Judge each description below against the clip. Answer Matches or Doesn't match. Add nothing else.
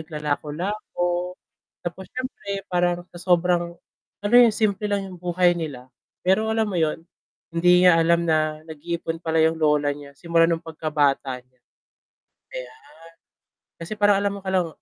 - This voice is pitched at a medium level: Matches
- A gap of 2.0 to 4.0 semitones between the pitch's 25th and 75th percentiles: Matches